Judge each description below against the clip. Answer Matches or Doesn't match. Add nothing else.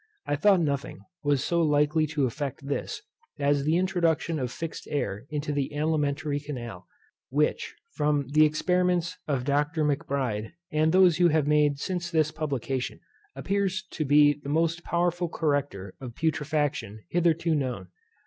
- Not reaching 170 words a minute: Matches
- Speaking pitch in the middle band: Matches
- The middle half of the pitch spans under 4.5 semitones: Matches